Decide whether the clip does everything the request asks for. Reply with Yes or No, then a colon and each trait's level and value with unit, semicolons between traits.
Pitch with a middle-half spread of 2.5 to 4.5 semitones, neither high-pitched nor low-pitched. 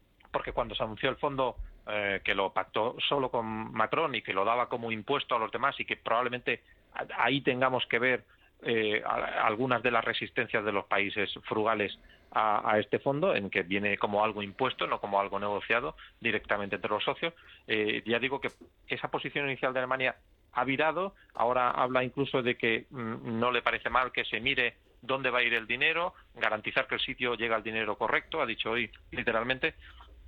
No: average, 3.3 semitones; low, 120 Hz